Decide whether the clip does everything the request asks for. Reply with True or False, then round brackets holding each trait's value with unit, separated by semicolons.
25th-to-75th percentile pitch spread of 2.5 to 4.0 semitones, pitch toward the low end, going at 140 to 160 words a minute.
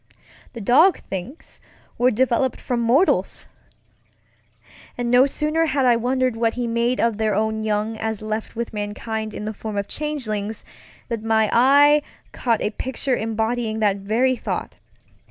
False (2.9 semitones; 230 Hz; 155 wpm)